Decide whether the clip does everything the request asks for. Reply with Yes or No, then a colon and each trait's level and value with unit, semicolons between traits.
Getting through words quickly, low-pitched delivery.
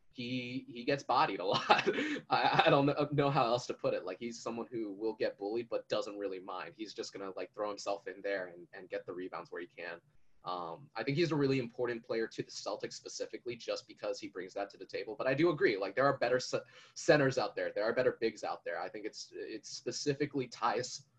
No: fast, 250 wpm; medium, 145 Hz